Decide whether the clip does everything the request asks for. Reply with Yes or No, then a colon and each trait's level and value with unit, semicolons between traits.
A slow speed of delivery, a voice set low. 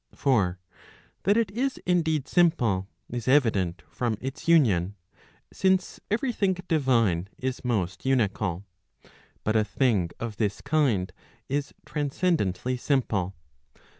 Yes: slow, 115 wpm; low, 125 Hz